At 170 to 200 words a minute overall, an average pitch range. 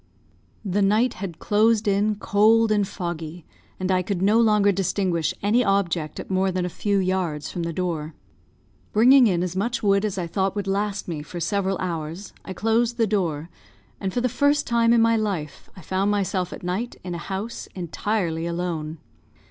Yes: average, 190 wpm; average, 3.4 semitones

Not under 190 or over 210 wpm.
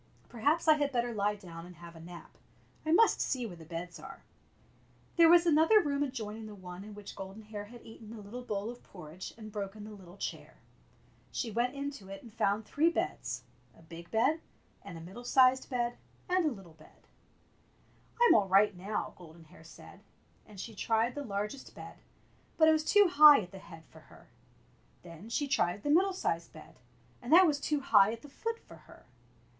Yes: fast, 205 wpm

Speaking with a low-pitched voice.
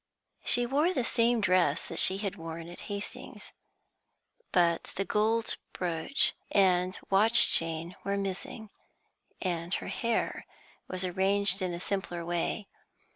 No: high, 190 Hz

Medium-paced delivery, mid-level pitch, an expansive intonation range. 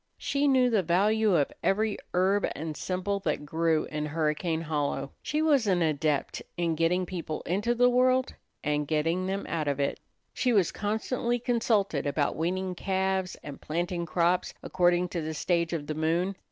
No: average, 170 wpm; medium, 175 Hz; average, 4.4 semitones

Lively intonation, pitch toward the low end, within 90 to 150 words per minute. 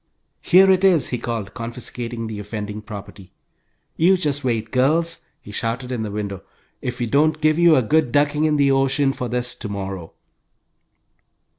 No: wide, 5.7 semitones; low, 125 Hz; average, 170 wpm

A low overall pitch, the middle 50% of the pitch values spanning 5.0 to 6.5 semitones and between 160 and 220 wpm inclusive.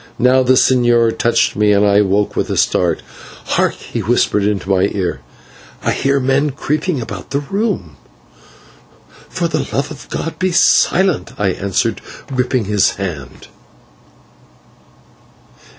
No: low, 115 Hz; wide, 5.4 semitones; slow, 135 wpm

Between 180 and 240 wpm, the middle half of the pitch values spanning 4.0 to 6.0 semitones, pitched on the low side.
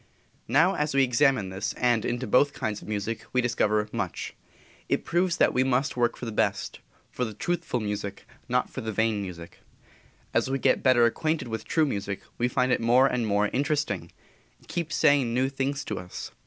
Yes: average, 200 wpm; average, 4.3 semitones; low, 125 Hz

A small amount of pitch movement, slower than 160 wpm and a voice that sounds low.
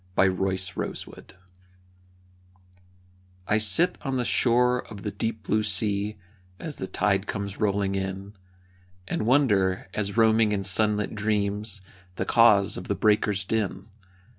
Yes: narrow, 2.1 semitones; slow, 135 wpm; low, 105 Hz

